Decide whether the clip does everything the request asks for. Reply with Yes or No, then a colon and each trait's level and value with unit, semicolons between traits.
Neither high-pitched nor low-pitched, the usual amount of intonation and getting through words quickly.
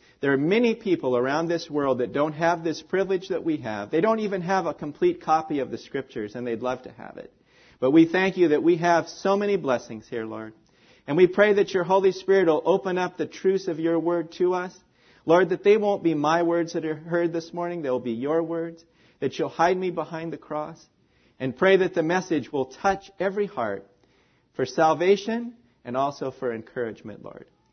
Yes: medium, 165 Hz; average, 4.4 semitones; fast, 215 wpm